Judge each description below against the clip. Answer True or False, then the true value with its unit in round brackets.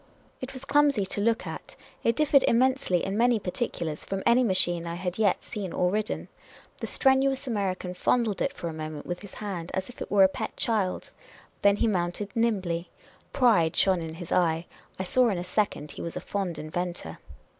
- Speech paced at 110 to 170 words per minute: False (200 wpm)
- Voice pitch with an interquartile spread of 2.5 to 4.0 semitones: False (4.9 semitones)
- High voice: True (195 Hz)